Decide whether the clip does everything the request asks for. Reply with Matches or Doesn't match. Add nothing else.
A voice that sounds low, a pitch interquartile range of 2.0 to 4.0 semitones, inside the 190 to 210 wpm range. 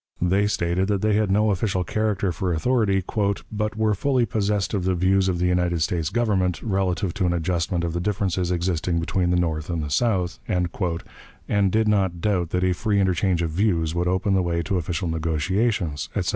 Matches